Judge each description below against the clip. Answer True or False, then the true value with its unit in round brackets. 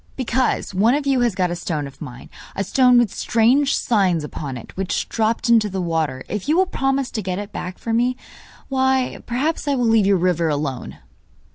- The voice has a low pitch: False (220 Hz)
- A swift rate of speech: True (210 wpm)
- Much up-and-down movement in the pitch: True (6.3 semitones)